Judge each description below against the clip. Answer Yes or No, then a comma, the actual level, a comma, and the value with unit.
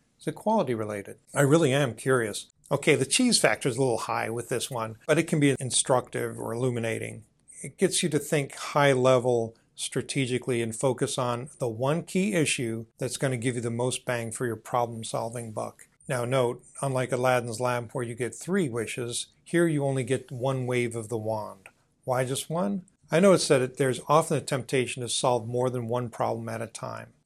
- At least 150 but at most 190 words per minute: No, fast, 205 wpm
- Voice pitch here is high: No, low, 130 Hz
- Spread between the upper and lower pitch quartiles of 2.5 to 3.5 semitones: Yes, average, 3.1 semitones